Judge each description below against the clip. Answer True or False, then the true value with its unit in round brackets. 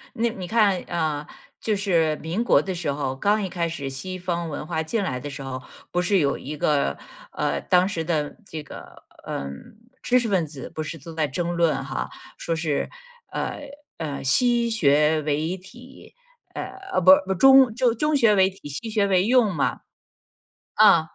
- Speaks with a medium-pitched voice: True (175 Hz)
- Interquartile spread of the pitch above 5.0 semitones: True (5.5 semitones)